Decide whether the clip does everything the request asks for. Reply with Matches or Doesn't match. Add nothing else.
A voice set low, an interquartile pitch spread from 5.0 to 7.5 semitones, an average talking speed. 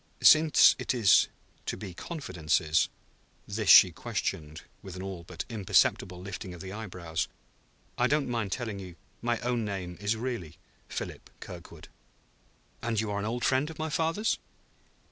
Matches